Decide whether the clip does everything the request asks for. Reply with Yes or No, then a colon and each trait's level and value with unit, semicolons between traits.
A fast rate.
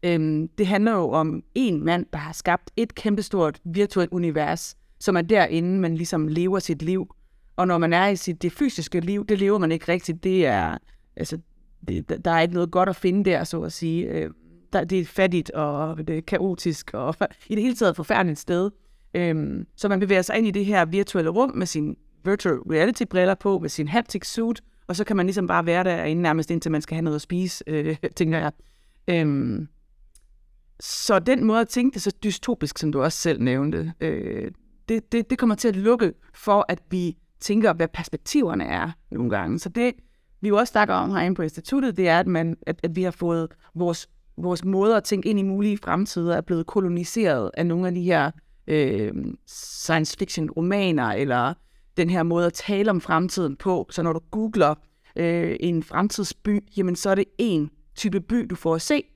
No: average, 200 wpm